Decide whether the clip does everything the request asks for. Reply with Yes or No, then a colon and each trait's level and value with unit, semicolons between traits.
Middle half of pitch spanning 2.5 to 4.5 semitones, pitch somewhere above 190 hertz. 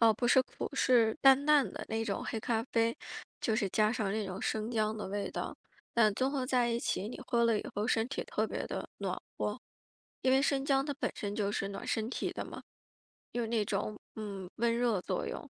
Yes: average, 2.8 semitones; high, 225 Hz